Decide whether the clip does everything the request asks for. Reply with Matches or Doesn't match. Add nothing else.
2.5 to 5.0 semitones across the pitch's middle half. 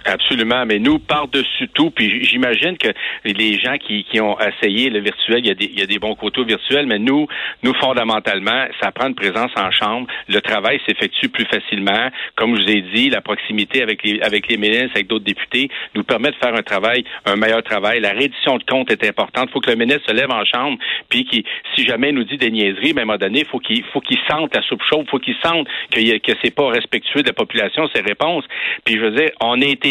Doesn't match